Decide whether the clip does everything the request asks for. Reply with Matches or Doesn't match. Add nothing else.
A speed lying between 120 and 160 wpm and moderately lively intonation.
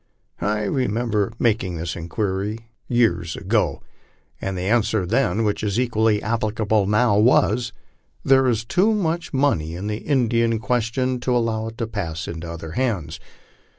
Matches